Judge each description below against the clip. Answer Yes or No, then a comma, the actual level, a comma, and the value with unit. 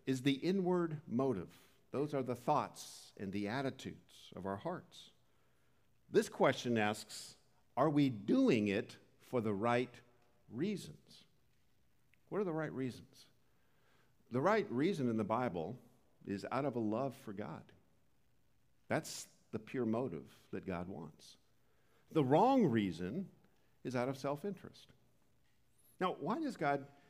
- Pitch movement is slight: No, average, 5.1 semitones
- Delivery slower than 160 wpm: Yes, slow, 135 wpm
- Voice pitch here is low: Yes, low, 130 Hz